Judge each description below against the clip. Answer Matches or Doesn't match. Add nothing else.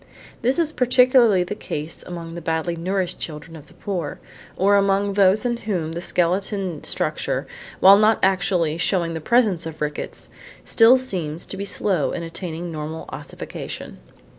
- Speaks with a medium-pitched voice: Matches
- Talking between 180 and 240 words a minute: Doesn't match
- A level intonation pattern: Doesn't match